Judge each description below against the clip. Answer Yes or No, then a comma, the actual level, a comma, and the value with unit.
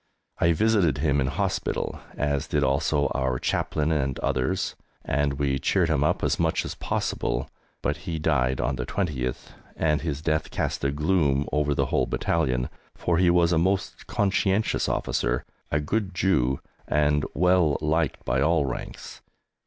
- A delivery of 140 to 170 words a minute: Yes, average, 160 wpm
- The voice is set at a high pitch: No, very low, 75 Hz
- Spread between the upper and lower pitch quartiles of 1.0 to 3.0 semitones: No, average, 3.6 semitones